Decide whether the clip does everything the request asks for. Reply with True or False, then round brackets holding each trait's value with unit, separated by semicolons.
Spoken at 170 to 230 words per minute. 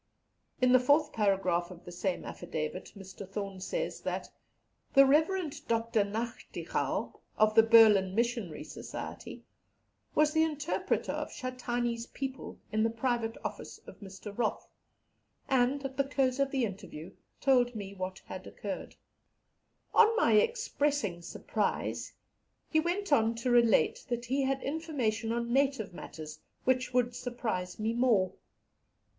False (140 wpm)